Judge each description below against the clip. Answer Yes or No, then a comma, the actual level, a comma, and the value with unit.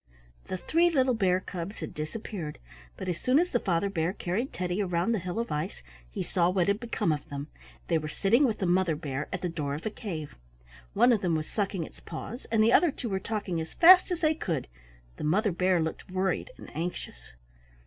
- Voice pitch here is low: No, medium, 185 Hz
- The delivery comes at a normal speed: No, fast, 220 wpm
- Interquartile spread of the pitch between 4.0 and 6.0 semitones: Yes, average, 5.2 semitones